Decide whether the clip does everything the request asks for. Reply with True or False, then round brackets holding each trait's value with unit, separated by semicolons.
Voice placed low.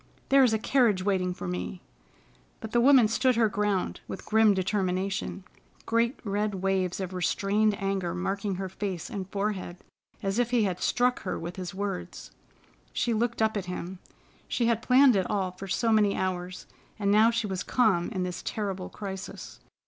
False (200 Hz)